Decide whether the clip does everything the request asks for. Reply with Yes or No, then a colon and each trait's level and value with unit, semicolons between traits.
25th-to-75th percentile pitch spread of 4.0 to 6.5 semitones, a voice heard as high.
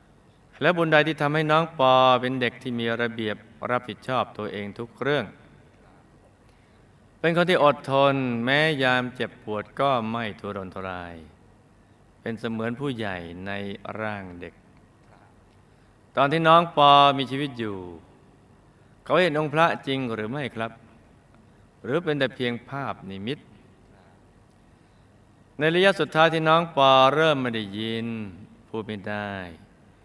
No: average, 4.9 semitones; low, 115 Hz